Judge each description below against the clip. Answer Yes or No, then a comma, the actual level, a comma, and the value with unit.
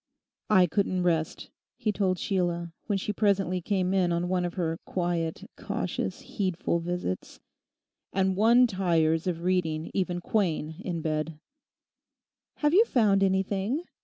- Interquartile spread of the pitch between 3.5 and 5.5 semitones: No, narrow, 2.5 semitones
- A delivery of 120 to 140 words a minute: Yes, slow, 135 wpm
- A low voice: No, medium, 185 Hz